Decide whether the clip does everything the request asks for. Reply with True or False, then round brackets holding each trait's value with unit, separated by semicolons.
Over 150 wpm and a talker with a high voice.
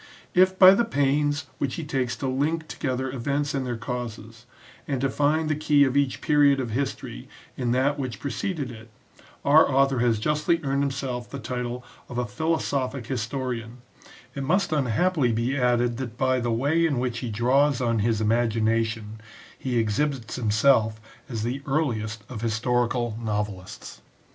False (165 wpm; 130 Hz)